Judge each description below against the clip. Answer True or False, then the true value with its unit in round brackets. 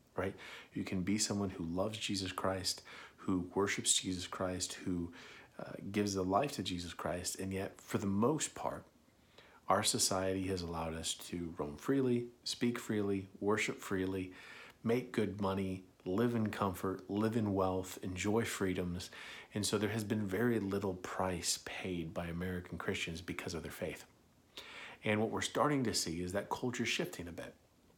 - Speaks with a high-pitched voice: False (95 Hz)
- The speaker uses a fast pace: False (165 wpm)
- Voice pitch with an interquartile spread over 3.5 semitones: False (2.6 semitones)